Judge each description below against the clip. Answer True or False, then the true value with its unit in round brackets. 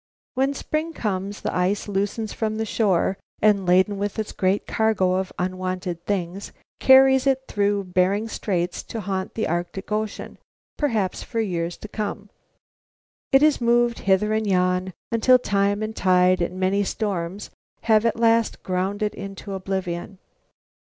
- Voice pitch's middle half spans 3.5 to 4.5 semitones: False (3.0 semitones)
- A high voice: True (200 Hz)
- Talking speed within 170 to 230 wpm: False (155 wpm)